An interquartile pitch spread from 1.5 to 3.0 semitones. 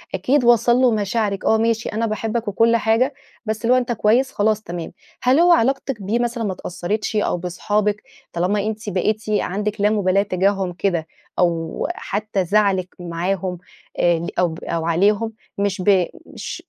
No: average, 3.5 semitones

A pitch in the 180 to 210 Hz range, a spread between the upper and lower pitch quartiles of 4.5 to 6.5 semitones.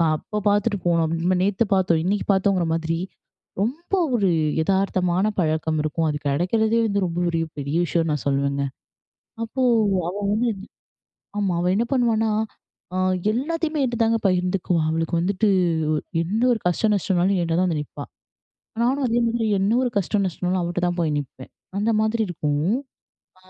Yes: medium, 185 Hz; average, 4.8 semitones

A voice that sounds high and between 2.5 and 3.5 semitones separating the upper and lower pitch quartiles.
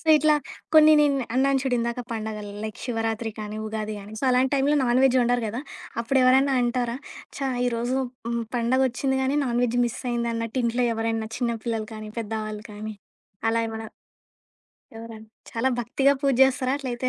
Yes: high, 240 Hz; average, 2.8 semitones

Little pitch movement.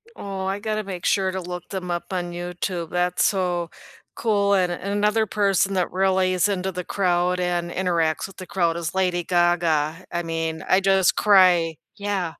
Yes: narrow, 1.8 semitones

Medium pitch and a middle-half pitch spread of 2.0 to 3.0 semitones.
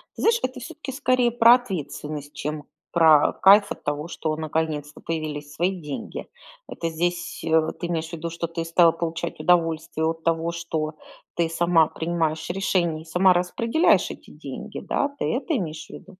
Yes: medium, 165 Hz; narrow, 2.5 semitones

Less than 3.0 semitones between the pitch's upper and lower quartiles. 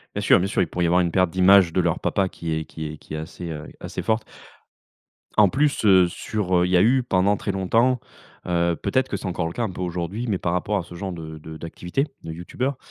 No: average, 3.4 semitones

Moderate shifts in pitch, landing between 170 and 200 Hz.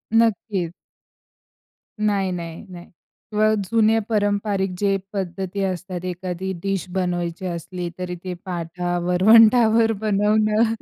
Yes: average, 3.1 semitones; high, 190 Hz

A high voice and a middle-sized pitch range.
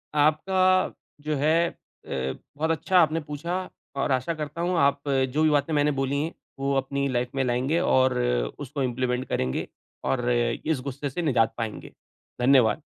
No: medium, 140 Hz; average, 3.6 semitones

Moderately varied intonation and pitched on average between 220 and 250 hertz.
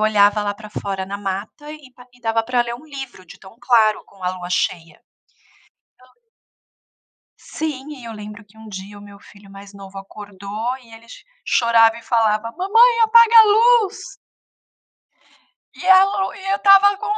No: wide, 7.1 semitones; high, 225 Hz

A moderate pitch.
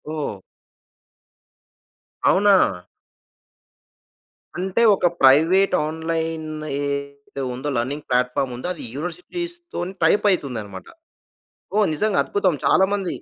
Yes: medium, 160 Hz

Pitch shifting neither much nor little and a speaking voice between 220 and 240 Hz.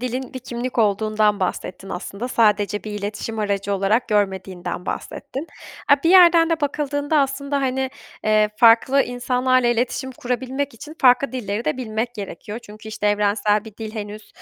Yes: average, 3.9 semitones; high, 230 Hz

